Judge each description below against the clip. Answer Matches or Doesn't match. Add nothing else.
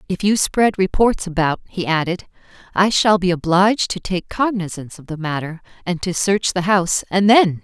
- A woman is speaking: Matches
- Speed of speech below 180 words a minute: Doesn't match